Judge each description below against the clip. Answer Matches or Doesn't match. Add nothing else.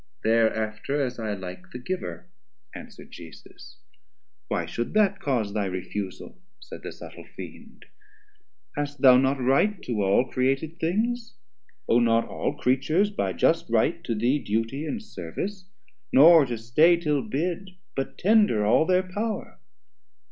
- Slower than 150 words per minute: Matches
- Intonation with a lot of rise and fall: Matches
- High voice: Doesn't match